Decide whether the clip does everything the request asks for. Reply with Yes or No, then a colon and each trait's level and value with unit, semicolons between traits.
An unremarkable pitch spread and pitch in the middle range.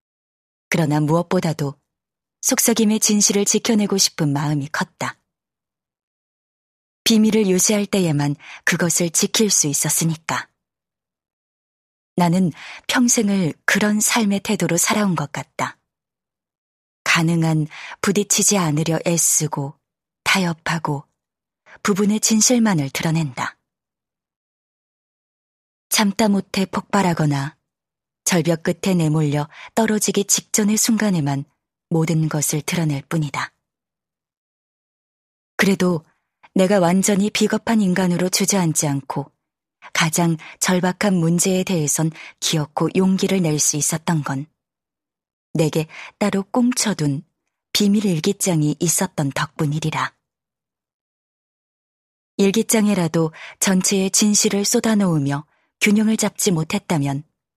Yes: average, 4.9 semitones; medium, 175 Hz